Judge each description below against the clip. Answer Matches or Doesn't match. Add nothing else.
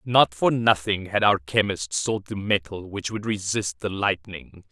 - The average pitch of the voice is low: Matches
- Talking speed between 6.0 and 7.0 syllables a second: Doesn't match